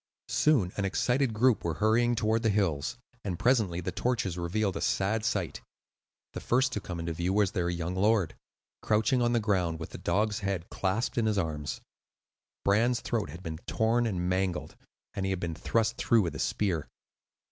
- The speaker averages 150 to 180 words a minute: No, average, 190 wpm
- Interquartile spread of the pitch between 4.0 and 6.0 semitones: Yes, average, 4.4 semitones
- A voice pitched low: Yes, low, 100 Hz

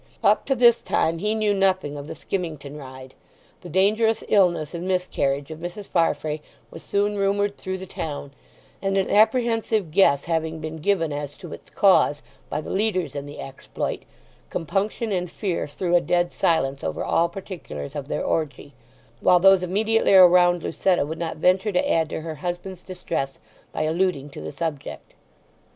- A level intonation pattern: No, average, 4.2 semitones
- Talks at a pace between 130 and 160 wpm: No, average, 170 wpm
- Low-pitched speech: No, medium, 175 Hz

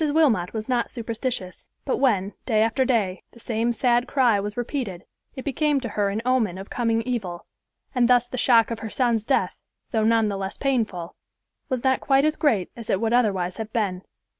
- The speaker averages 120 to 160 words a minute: No, average, 200 wpm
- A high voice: Yes, high, 230 Hz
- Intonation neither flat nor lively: Yes, average, 3.6 semitones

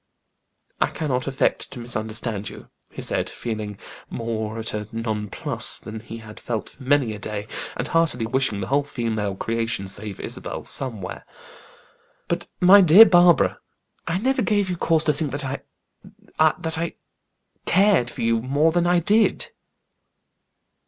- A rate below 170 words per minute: Yes, average, 150 wpm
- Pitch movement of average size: No, wide, 6.9 semitones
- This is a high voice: No, low, 125 Hz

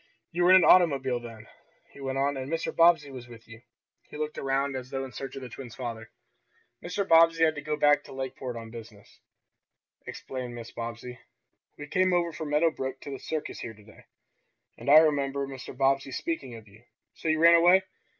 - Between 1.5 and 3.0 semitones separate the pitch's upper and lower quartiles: No, average, 4.3 semitones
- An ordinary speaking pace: No, fast, 210 wpm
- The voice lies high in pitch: No, low, 135 Hz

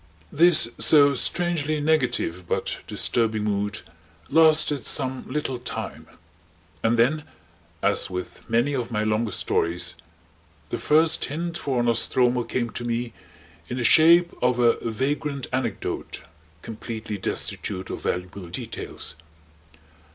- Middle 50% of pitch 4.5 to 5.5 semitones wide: Yes, average, 5.1 semitones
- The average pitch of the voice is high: No, low, 125 Hz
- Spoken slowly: Yes, slow, 120 wpm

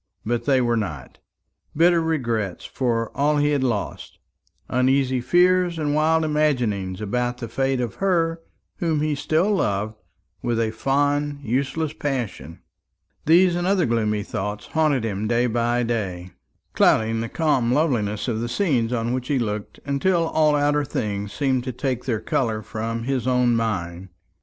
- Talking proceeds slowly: No, average, 155 wpm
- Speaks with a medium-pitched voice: No, low, 125 Hz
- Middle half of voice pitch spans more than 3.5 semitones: Yes, average, 4.8 semitones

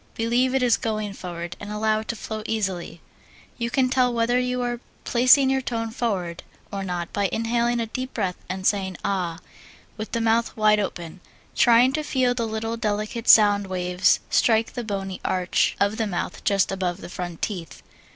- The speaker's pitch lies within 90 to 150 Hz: No, high, 215 Hz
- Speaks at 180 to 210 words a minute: Yes, average, 185 wpm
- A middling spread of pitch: Yes, average, 3.8 semitones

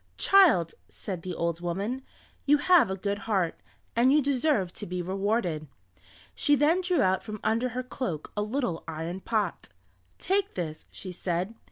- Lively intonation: Yes, wide, 7.0 semitones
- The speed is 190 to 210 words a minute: No, average, 165 wpm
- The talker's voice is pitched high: Yes, high, 205 Hz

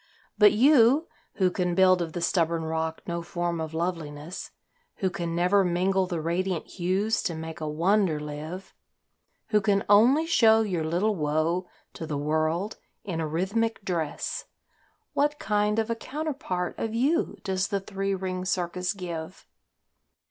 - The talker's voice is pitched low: No, medium, 185 Hz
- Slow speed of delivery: No, average, 155 wpm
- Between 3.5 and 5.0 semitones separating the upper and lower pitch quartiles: Yes, average, 3.9 semitones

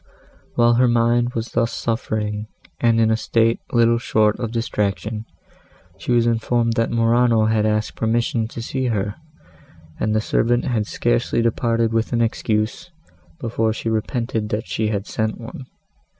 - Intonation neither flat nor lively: No, narrow, 1.4 semitones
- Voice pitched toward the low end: Yes, low, 115 Hz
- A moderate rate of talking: Yes, average, 150 wpm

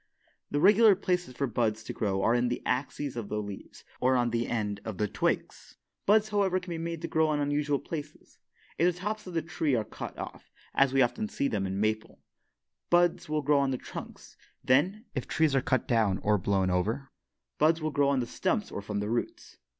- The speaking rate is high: Yes, fast, 220 wpm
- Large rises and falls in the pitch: Yes, wide, 7.0 semitones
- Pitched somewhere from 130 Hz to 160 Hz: Yes, medium, 140 Hz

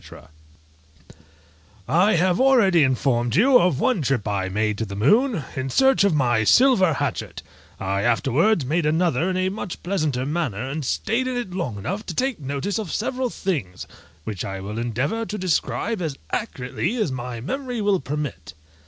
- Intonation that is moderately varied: No, wide, 8.9 semitones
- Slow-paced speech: No, average, 170 wpm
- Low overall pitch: No, medium, 160 Hz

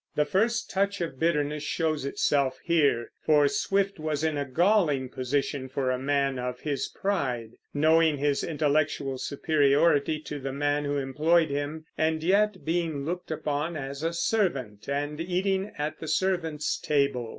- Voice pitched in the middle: Yes, medium, 150 Hz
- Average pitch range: Yes, average, 3.0 semitones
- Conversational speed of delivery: Yes, average, 155 wpm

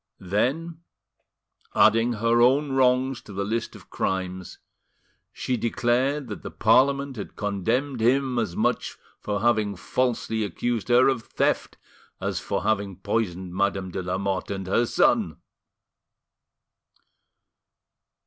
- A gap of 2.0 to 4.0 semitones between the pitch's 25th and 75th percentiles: No, average, 4.4 semitones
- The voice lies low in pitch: Yes, low, 115 Hz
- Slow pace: Yes, slow, 120 wpm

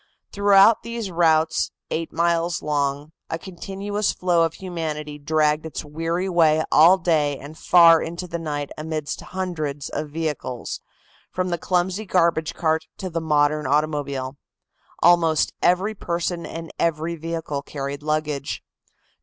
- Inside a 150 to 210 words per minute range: No, slow, 135 wpm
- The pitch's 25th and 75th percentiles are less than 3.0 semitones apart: Yes, narrow, 2.5 semitones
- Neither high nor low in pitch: Yes, medium, 165 Hz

